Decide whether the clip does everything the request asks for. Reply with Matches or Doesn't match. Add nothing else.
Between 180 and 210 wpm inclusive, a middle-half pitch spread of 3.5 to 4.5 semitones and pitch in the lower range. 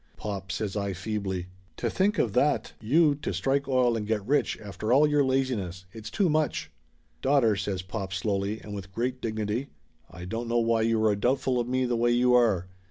Matches